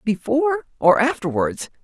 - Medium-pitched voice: No, very high, 265 Hz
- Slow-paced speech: Yes, slow, 100 wpm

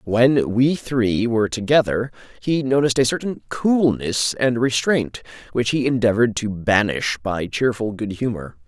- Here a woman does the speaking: No, male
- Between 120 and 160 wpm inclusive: Yes, average, 145 wpm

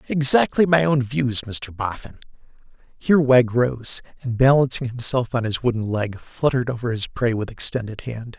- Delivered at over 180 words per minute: No, average, 165 wpm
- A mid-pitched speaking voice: No, low, 125 Hz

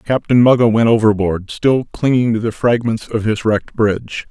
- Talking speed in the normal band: Yes, average, 180 wpm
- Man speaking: Yes, male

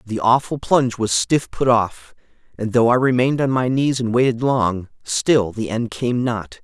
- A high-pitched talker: No, low, 120 Hz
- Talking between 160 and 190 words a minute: No, average, 200 wpm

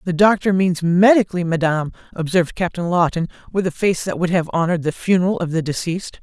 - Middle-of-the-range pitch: Yes, medium, 175 Hz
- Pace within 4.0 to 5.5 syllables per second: No, 6.2 syllables/s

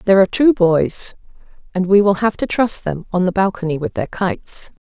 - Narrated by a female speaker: Yes, female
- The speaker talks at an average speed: No, fast, 210 wpm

